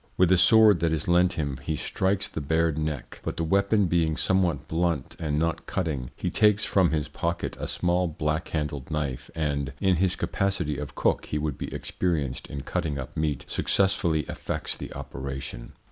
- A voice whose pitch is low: Yes, very low, 80 Hz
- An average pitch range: Yes, average, 3.5 semitones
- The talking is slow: No, average, 185 wpm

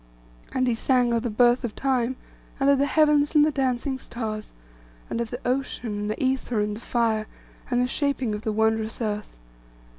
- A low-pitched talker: No, high, 240 Hz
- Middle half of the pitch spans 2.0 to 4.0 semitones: Yes, average, 3.2 semitones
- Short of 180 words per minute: No, average, 200 wpm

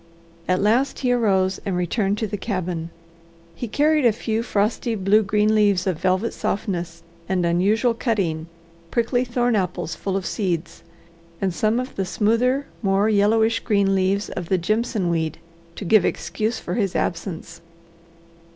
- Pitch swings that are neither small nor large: Yes, average, 3.5 semitones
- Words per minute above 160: No, average, 155 wpm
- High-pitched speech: Yes, high, 205 Hz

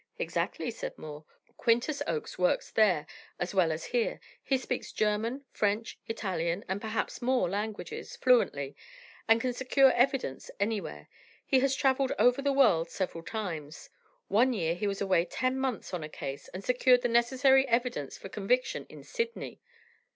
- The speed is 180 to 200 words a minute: No, average, 160 wpm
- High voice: Yes, high, 230 Hz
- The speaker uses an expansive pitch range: Yes, wide, 6.0 semitones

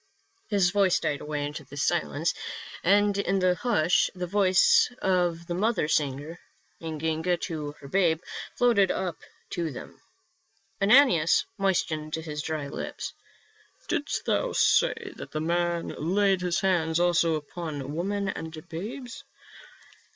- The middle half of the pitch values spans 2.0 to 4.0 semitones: Yes, average, 3.5 semitones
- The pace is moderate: No, slow, 130 wpm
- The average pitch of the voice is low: No, medium, 170 Hz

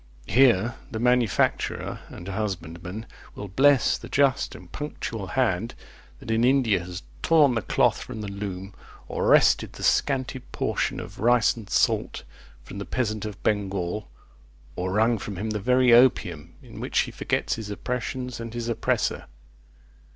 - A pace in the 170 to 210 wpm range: No, average, 155 wpm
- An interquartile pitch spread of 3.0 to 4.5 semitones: Yes, average, 4.1 semitones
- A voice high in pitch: No, low, 110 Hz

